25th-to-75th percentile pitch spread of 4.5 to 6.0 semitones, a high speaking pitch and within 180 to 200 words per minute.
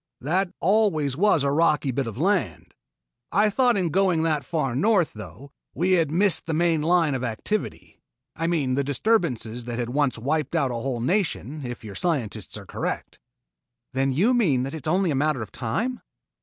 No: wide, 5.6 semitones; medium, 155 Hz; average, 195 wpm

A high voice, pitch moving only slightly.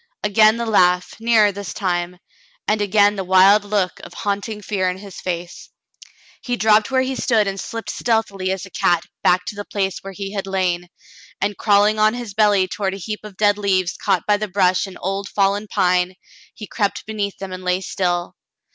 Yes: high, 200 Hz; narrow, 2.2 semitones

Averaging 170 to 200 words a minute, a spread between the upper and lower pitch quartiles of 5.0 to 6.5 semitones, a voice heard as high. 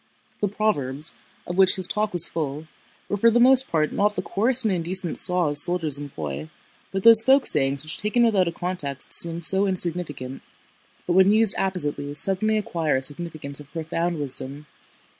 No: average, 175 wpm; wide, 5.4 semitones; medium, 175 Hz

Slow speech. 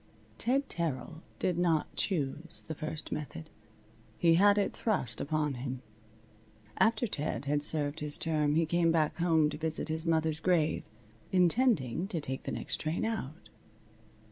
No: average, 150 wpm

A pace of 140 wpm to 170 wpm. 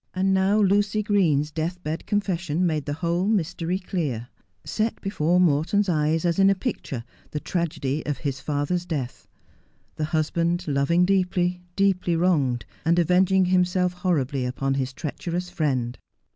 Yes: average, 145 wpm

